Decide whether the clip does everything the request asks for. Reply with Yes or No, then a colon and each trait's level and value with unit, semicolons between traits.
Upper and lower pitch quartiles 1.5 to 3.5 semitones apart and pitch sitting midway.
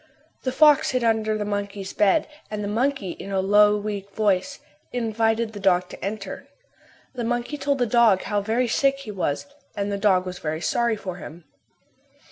No: average, 3.2 semitones; high, 210 Hz